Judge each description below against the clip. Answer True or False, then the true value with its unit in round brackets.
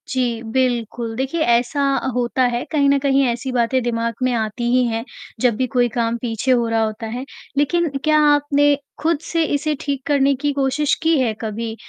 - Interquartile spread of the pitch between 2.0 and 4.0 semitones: True (3.4 semitones)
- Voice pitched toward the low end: False (255 Hz)